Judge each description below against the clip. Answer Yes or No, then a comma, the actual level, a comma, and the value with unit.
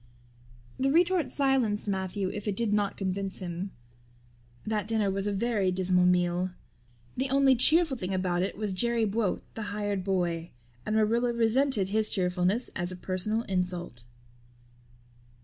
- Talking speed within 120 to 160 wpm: Yes, average, 150 wpm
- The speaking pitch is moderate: No, high, 200 Hz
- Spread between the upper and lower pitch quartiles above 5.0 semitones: No, average, 3.9 semitones